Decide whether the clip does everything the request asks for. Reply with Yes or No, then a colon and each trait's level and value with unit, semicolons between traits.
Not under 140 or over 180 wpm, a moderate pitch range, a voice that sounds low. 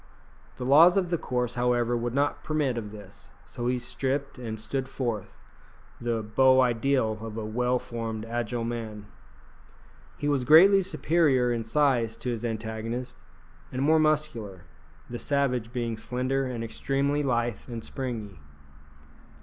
Yes: average, 145 wpm; average, 3.2 semitones; low, 125 Hz